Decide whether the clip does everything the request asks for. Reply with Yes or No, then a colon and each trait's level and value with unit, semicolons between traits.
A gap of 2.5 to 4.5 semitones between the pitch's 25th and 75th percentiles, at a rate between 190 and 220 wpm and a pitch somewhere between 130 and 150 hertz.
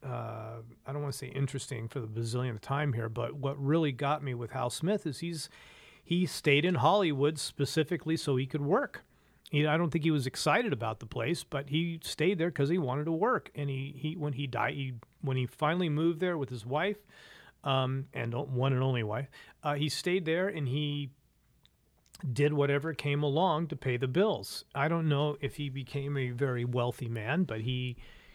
Yes: average, 3.4 semitones; fast, 205 wpm; medium, 140 Hz